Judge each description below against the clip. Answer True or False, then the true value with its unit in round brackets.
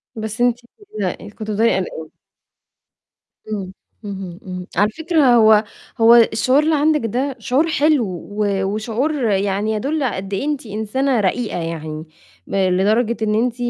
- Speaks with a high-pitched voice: True (220 Hz)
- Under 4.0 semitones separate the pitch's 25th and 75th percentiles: False (4.6 semitones)